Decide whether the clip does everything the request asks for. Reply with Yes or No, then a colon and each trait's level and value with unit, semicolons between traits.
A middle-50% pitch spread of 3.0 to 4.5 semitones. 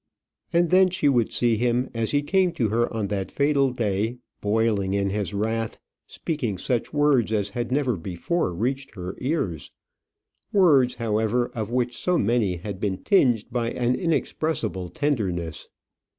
No: average, 5.2 semitones